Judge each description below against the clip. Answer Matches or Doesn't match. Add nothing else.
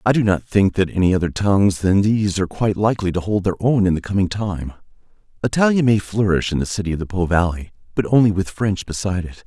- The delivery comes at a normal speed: Doesn't match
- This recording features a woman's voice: Doesn't match